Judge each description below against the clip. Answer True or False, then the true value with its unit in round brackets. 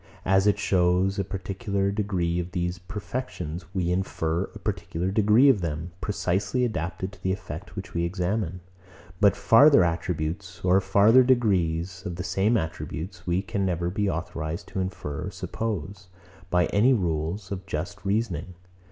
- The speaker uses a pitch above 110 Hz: False (95 Hz)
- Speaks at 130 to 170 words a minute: True (155 wpm)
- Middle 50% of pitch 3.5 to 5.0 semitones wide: False (2.7 semitones)